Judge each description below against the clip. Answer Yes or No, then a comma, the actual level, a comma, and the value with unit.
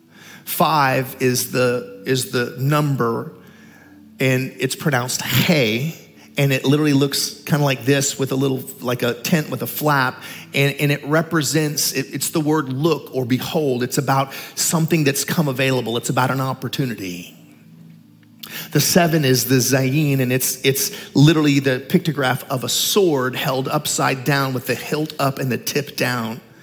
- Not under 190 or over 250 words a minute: No, average, 165 wpm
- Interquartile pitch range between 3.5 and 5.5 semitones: No, average, 2.8 semitones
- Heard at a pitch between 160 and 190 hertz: No, low, 135 Hz